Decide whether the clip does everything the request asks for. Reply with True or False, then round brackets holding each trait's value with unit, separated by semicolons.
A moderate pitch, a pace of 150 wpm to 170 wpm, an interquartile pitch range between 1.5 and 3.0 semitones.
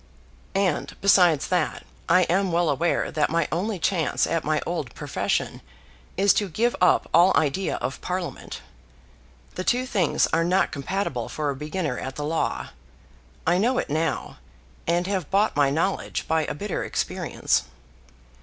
False (170 Hz; 155 wpm; 3.8 semitones)